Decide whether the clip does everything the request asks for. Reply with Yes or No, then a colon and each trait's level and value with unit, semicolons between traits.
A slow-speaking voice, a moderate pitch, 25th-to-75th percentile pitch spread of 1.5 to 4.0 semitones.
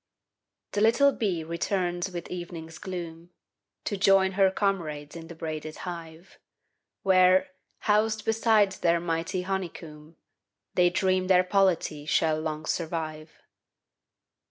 Yes: slow, 115 wpm; medium, 175 Hz; average, 3.0 semitones